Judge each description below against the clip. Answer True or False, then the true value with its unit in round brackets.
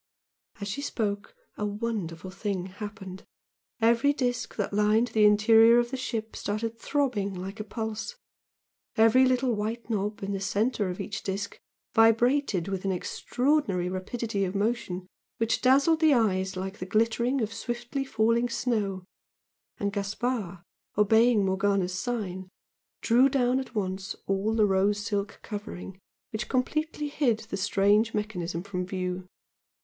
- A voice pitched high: True (210 Hz)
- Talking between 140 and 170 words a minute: True (145 wpm)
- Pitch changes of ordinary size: True (3.4 semitones)